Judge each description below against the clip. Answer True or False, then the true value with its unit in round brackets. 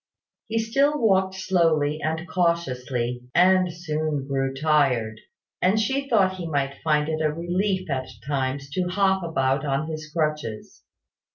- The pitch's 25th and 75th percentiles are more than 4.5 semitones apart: True (5.2 semitones)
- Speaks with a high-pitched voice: False (155 Hz)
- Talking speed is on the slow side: False (145 wpm)